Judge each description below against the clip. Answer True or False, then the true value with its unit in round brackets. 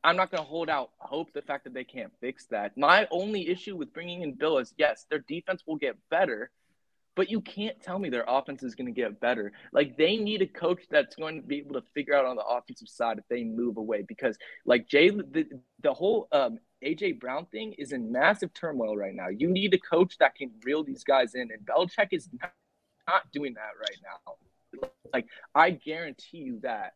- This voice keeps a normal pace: False (225 wpm)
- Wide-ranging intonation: True (6.8 semitones)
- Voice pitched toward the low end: False (170 Hz)